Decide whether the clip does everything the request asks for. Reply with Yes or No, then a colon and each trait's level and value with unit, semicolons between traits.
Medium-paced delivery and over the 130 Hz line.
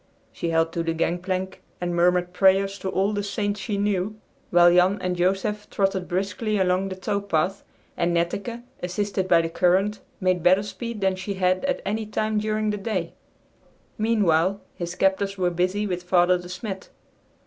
Yes: average, 175 wpm; high, 190 Hz